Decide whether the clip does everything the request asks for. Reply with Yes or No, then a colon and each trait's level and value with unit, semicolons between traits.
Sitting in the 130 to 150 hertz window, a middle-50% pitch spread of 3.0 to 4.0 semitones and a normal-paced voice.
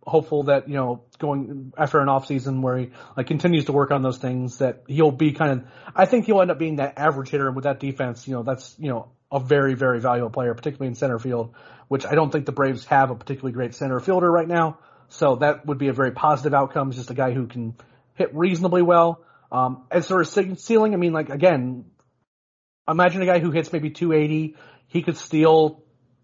No: medium, 140 Hz; average, 3.7 semitones; fast, 230 wpm